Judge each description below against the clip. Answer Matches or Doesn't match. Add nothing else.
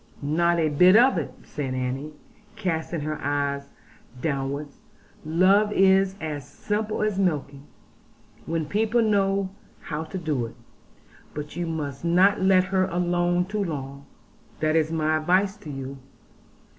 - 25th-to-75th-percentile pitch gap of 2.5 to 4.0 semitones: Doesn't match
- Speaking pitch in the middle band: Matches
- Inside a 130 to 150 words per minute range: Matches